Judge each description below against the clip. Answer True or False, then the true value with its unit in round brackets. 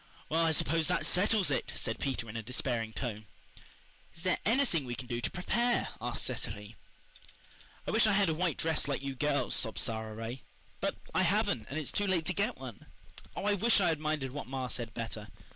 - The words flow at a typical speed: False (210 wpm)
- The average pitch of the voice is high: False (140 Hz)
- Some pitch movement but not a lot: False (7.4 semitones)